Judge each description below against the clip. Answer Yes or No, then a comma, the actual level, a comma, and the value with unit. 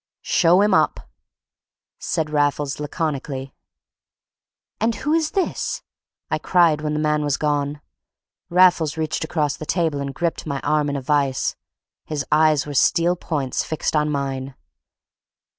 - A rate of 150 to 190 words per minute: No, average, 140 wpm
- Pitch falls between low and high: Yes, medium, 150 Hz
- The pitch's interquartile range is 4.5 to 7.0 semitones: No, narrow, 2.4 semitones